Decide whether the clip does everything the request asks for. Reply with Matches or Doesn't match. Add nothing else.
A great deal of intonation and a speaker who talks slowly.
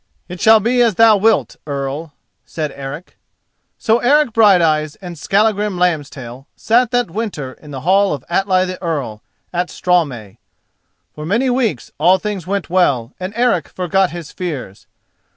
Doesn't match